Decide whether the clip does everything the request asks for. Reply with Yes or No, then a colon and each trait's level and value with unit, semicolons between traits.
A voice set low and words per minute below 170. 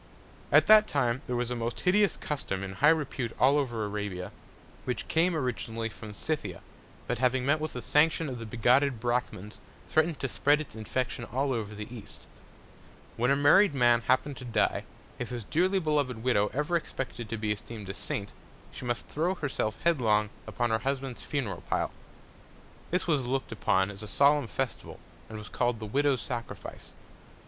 No: low, 125 Hz; average, 180 wpm